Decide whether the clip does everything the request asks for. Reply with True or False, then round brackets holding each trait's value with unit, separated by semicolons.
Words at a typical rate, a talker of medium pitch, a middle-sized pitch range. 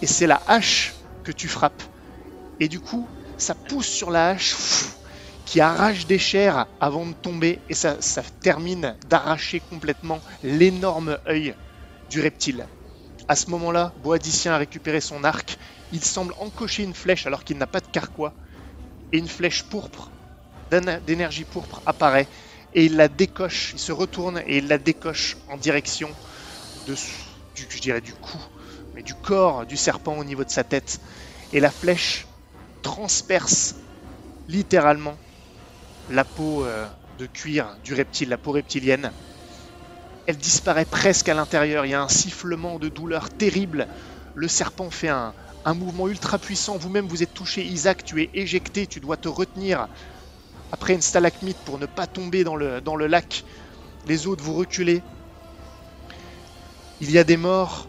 True (160 wpm; 160 Hz; 4.4 semitones)